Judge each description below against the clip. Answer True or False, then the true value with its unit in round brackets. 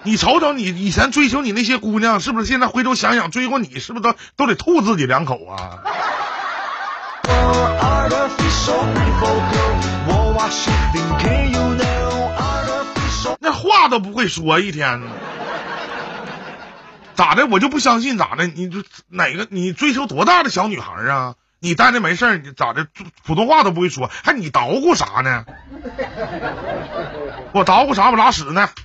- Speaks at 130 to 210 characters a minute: True (200 characters per minute)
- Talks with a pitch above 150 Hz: True (185 Hz)